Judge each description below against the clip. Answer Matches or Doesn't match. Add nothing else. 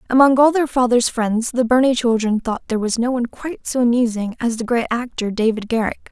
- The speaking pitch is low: Doesn't match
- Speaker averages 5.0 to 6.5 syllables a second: Matches